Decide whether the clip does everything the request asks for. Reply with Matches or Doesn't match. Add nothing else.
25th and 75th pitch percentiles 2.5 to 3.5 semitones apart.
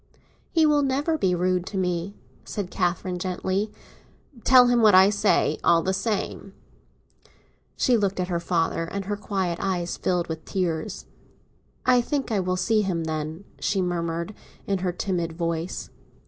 Matches